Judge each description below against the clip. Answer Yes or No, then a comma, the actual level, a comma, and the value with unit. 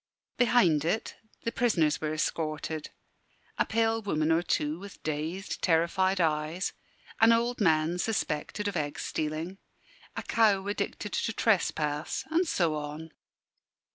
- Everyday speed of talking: No, slow, 130 wpm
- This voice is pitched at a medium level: Yes, medium, 170 Hz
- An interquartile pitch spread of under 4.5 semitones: No, average, 5.1 semitones